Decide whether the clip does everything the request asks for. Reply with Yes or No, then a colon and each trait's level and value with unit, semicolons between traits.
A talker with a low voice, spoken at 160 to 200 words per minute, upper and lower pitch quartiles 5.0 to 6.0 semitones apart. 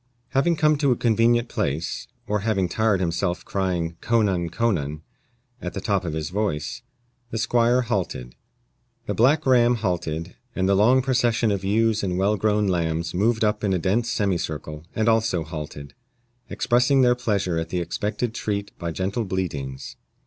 Yes: low, 100 Hz; average, 170 wpm; average, 5.3 semitones